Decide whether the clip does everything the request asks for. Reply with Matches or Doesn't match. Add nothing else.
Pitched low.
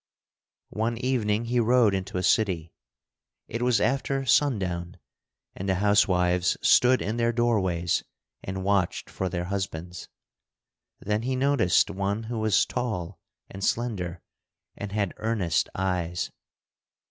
Matches